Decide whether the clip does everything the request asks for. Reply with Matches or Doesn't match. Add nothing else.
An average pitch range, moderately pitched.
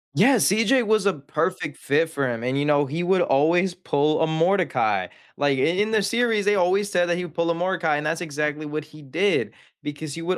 Matches